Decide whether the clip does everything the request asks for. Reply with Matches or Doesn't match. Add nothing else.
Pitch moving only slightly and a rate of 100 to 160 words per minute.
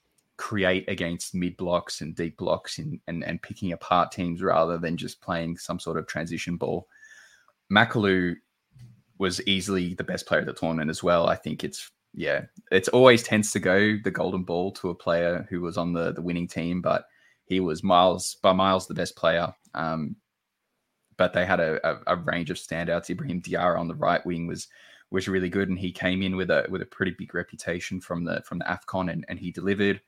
Doesn't match